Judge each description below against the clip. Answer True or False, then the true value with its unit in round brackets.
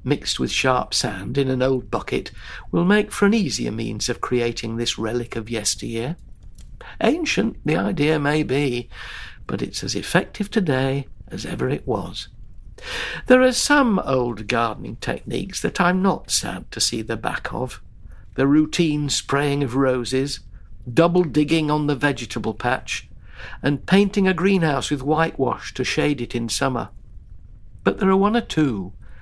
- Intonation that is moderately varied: False (6.3 semitones)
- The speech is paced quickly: False (160 wpm)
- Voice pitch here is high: False (140 Hz)